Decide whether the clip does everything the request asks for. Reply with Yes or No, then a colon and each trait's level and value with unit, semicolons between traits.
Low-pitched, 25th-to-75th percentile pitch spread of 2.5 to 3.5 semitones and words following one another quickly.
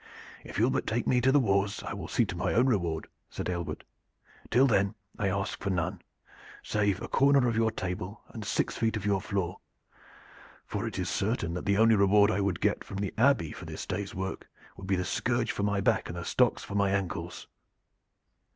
Yes: low, 100 Hz; average, 3.2 semitones; fast, 215 wpm